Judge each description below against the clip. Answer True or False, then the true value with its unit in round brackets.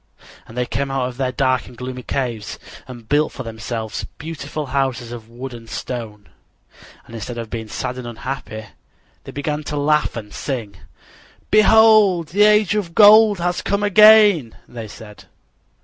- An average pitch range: False (6.5 semitones)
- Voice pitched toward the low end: True (130 Hz)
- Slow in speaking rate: False (165 wpm)